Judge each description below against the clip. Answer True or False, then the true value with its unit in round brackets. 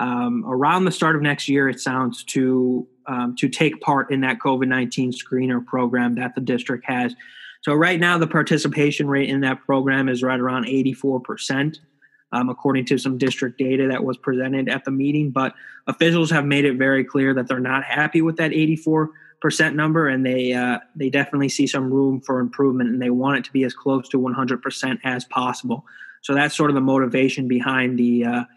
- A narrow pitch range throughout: True (2.0 semitones)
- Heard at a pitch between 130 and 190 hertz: True (135 Hz)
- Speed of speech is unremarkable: False (210 wpm)